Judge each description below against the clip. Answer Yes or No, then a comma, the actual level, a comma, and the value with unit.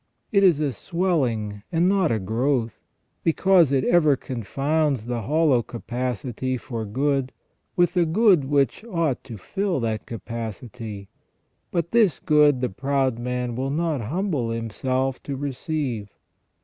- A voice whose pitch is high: No, low, 135 Hz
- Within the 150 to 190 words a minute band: No, slow, 135 wpm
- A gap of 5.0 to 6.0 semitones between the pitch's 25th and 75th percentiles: Yes, average, 5.3 semitones